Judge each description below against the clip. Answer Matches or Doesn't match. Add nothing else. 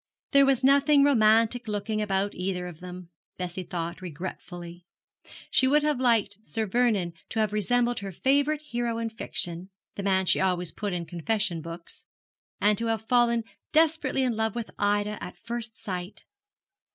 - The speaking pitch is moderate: Doesn't match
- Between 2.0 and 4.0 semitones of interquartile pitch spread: Doesn't match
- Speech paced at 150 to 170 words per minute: Matches